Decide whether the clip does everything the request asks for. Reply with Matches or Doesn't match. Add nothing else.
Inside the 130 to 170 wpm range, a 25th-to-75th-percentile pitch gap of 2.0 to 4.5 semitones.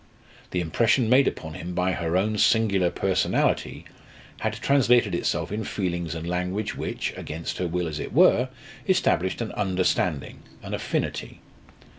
Matches